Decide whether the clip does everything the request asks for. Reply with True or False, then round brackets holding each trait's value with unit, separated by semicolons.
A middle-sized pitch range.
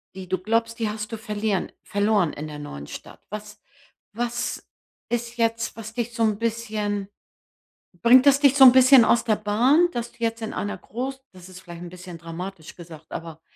True (4.0 semitones)